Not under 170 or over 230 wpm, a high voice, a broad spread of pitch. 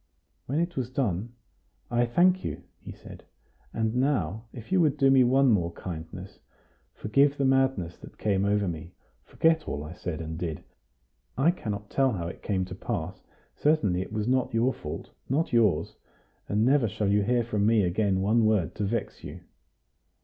No: average, 180 wpm; low, 110 Hz; wide, 6.0 semitones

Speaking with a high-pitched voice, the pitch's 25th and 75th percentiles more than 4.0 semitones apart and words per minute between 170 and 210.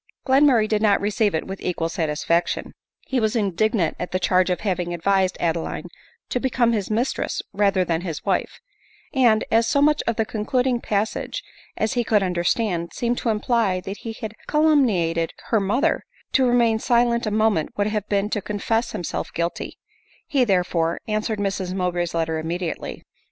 Yes: high, 210 Hz; average, 4.5 semitones; average, 180 wpm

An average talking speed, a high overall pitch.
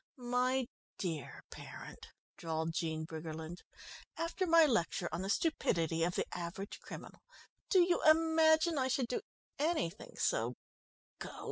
No: slow, 130 wpm; high, 220 Hz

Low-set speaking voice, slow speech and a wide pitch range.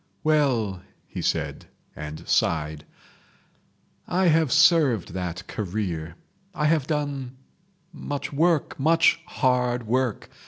Yes: low, 130 Hz; slow, 95 wpm; wide, 7.7 semitones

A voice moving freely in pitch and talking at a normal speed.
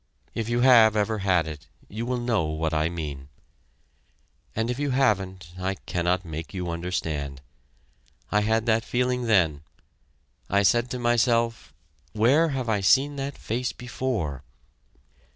Yes: wide, 6.0 semitones; average, 145 wpm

